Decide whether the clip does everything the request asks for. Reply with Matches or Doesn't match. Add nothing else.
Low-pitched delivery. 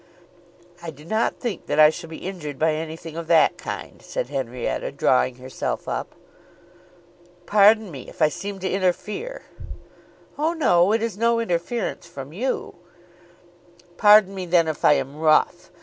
Doesn't match